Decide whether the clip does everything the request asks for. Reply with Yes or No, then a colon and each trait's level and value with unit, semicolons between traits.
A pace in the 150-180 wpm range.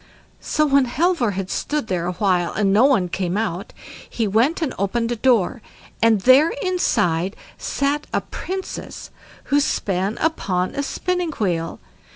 Yes: average, 155 wpm